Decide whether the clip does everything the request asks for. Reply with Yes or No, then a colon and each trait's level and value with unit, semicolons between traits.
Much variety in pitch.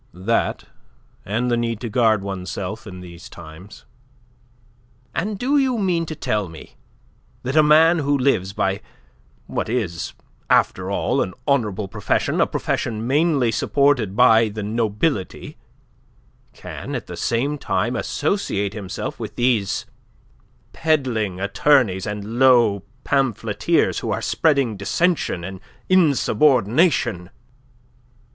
Yes: wide, 6.2 semitones